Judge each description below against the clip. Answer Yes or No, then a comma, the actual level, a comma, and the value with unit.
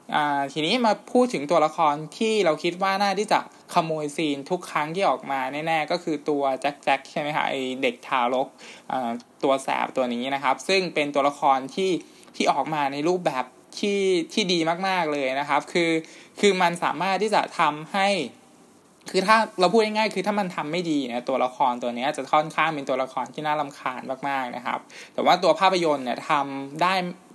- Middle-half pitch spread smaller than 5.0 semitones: No, wide, 5.5 semitones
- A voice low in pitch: No, medium, 155 Hz